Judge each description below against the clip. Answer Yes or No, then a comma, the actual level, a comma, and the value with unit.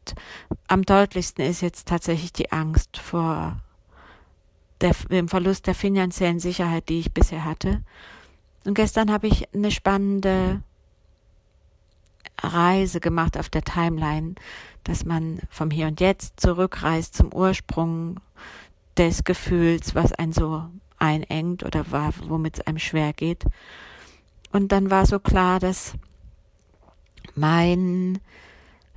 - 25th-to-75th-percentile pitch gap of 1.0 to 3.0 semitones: No, average, 5.1 semitones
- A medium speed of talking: No, slow, 115 wpm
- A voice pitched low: No, medium, 165 Hz